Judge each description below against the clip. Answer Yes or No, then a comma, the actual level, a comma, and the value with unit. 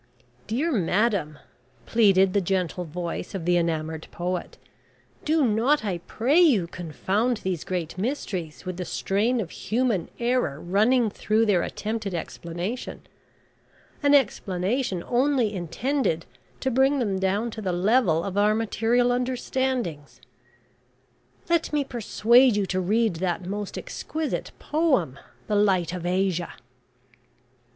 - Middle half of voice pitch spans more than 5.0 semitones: Yes, wide, 5.5 semitones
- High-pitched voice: Yes, high, 205 Hz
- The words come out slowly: Yes, slow, 130 wpm